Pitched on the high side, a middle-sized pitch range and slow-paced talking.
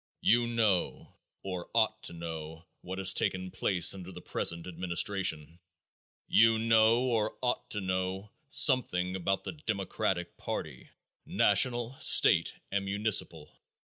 No: very low, 95 Hz; average, 4.0 semitones; slow, 125 wpm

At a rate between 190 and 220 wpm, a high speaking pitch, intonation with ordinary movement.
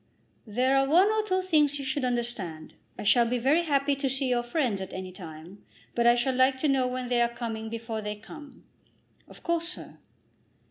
Yes: fast, 205 wpm; very high, 250 Hz; average, 3.9 semitones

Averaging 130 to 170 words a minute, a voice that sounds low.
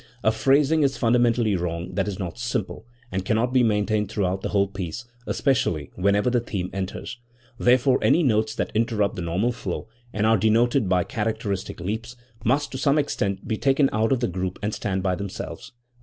No: average, 185 wpm; low, 110 Hz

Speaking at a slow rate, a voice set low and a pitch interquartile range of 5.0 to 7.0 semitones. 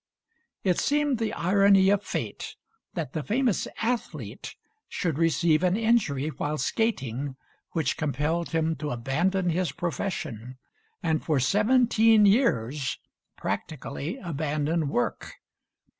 No: slow, 115 wpm; medium, 165 Hz; wide, 5.6 semitones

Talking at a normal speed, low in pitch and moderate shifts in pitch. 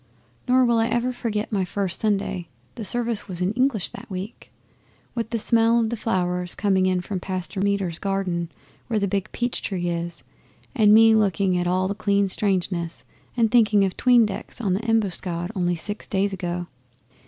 No: average, 185 wpm; high, 200 Hz; average, 3.6 semitones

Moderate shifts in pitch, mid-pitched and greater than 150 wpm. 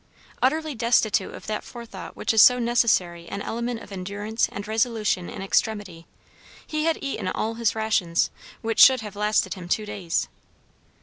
No: average, 3.0 semitones; high, 220 Hz; average, 165 wpm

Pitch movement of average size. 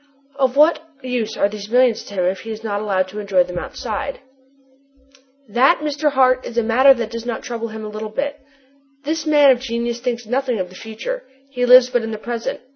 Yes: average, 3.5 semitones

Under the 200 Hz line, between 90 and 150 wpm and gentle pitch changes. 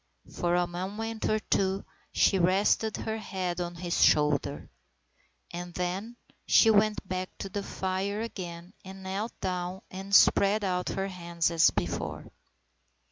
Yes: high, 190 Hz; average, 140 wpm; narrow, 2.3 semitones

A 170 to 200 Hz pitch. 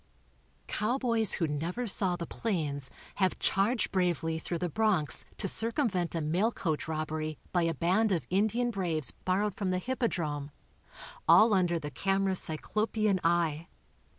Yes: medium, 185 Hz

